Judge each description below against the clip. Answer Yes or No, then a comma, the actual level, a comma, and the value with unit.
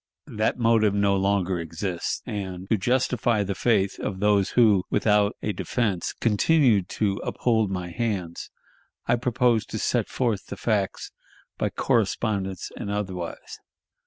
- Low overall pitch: Yes, low, 105 Hz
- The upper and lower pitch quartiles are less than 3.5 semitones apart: Yes, average, 2.9 semitones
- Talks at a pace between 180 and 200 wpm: No, slow, 135 wpm